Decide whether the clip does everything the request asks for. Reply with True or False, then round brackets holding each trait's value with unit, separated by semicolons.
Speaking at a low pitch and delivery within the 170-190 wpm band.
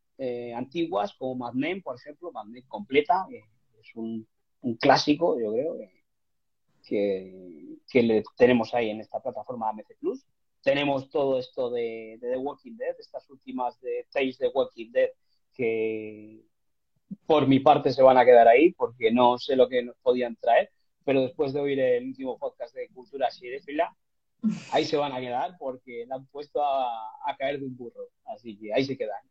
True (130 Hz; 185 wpm)